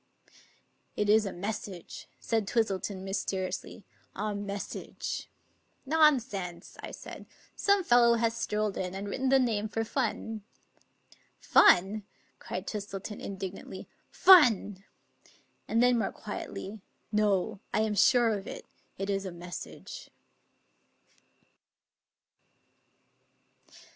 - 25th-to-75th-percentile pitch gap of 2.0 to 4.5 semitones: Yes, average, 2.8 semitones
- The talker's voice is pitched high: Yes, high, 210 Hz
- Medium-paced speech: No, slow, 115 wpm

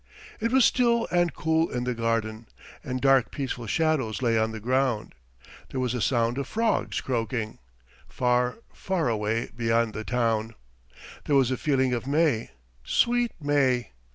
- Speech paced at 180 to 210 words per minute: No, average, 155 wpm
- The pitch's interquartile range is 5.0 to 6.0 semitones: No, average, 4.1 semitones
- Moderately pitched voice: No, low, 125 Hz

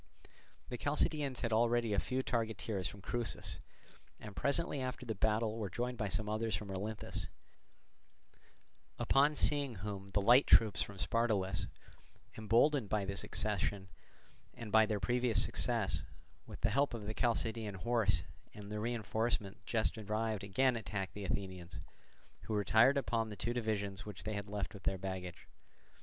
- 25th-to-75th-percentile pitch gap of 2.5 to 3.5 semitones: Yes, average, 3.1 semitones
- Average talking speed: Yes, average, 155 wpm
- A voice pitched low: Yes, low, 110 Hz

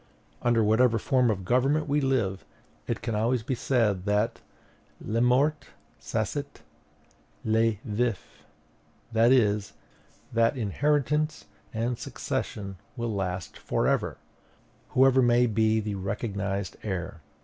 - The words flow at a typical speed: No, slow, 115 wpm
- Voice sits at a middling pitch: No, low, 115 Hz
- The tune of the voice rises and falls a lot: No, average, 3.5 semitones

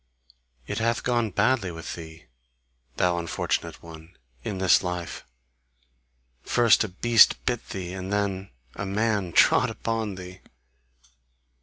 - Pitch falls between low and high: No, very low, 95 Hz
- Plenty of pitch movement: No, average, 3.9 semitones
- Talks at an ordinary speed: No, slow, 125 wpm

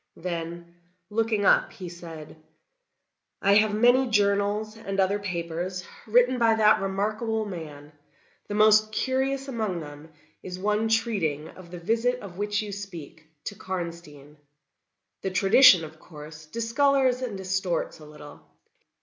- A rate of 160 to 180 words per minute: No, slow, 135 wpm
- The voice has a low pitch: No, high, 200 Hz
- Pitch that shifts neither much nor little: Yes, average, 4.5 semitones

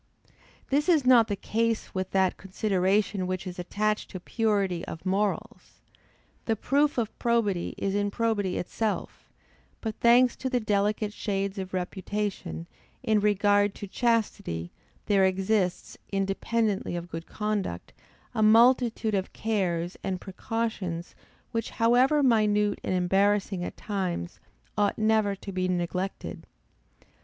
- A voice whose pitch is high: Yes, high, 205 Hz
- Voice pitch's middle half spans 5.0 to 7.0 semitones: No, average, 3.0 semitones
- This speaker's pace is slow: Yes, slow, 130 wpm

